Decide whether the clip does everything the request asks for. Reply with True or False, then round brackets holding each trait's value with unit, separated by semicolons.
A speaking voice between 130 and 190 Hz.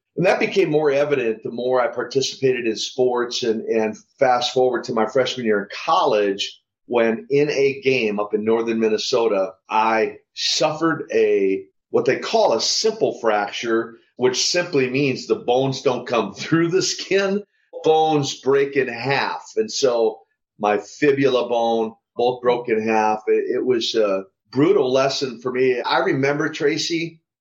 True (135 Hz)